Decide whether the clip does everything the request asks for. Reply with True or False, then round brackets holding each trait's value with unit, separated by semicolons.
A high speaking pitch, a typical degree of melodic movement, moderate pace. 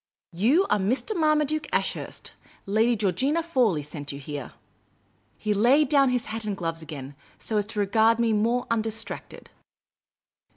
True (220 Hz; 4.9 semitones; 160 wpm)